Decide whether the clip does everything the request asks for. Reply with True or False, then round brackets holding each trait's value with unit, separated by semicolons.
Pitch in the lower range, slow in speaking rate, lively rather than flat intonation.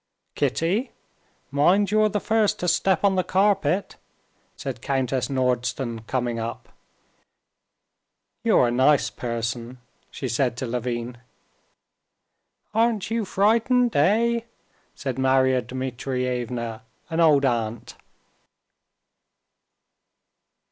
True (130 Hz; 95 wpm; 8.0 semitones)